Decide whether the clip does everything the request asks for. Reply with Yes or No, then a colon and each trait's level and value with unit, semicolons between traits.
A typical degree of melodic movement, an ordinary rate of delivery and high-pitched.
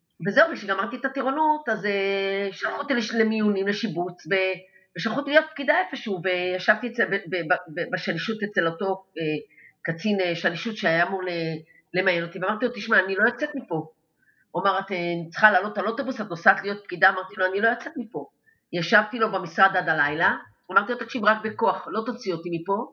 No: average, 4.0 semitones; fast, 185 wpm; high, 195 Hz